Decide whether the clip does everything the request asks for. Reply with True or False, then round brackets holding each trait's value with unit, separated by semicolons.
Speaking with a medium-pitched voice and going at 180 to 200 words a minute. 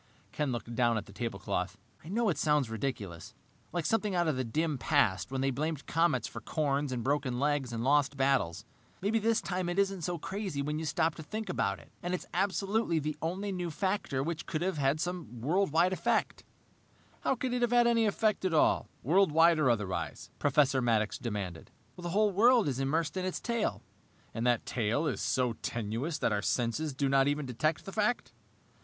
True (150 Hz; 195 wpm)